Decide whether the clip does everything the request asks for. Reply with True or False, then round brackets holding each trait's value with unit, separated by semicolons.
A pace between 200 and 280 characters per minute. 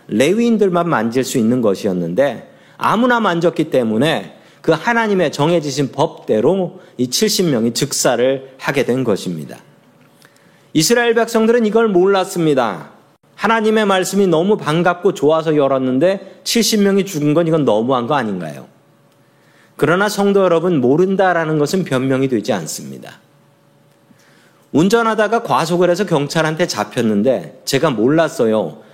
False (305 characters per minute)